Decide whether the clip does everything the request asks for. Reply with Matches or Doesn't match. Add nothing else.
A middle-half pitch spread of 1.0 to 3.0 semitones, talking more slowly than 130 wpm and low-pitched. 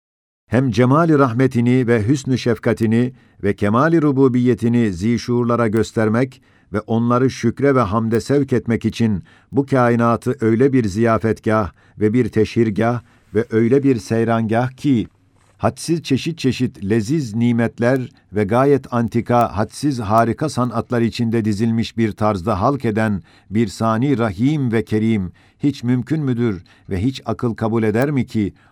Doesn't match